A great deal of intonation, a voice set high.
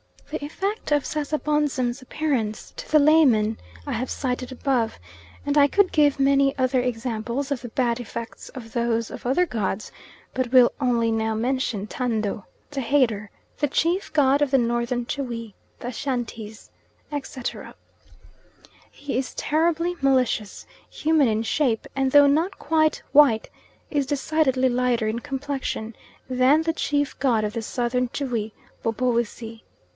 No: average, 3.8 semitones; very high, 255 Hz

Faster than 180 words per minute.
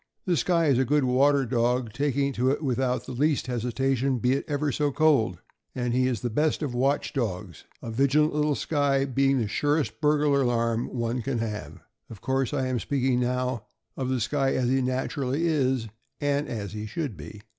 Yes: average, 200 wpm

